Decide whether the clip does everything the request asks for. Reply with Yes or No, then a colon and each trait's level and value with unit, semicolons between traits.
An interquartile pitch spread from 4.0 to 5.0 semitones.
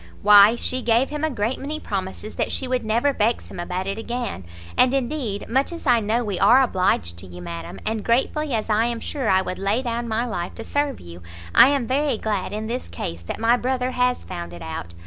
Yes: average, 4.6 semitones